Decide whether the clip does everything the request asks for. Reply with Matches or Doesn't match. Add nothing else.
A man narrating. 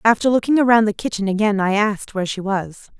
Doesn't match